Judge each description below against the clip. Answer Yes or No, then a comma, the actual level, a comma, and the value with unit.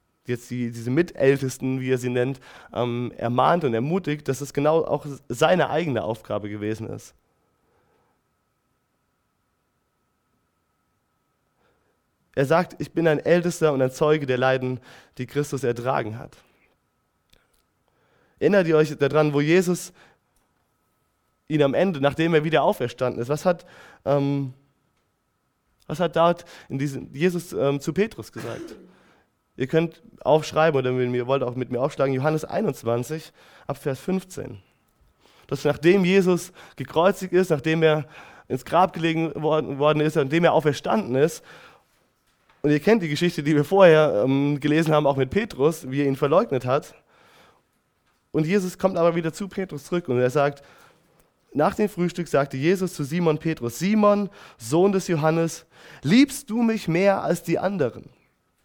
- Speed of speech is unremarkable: Yes, average, 145 wpm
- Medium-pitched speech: Yes, medium, 150 Hz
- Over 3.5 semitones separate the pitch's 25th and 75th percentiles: Yes, average, 4.3 semitones